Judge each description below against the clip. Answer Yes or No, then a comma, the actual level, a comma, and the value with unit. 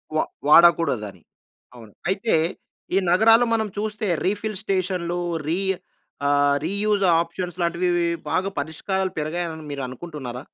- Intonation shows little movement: No, average, 4.4 semitones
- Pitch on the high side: No, medium, 175 Hz